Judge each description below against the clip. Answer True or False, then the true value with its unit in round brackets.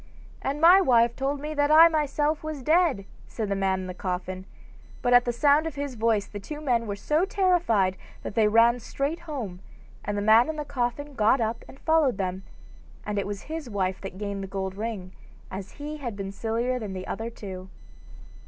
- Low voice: False (235 Hz)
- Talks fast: True (210 wpm)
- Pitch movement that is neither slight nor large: False (6.8 semitones)